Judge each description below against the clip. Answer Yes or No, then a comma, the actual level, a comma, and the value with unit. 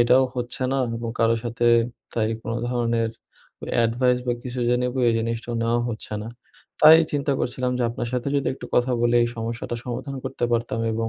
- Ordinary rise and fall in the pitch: No, narrow, 1.5 semitones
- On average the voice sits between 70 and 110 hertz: No, low, 120 Hz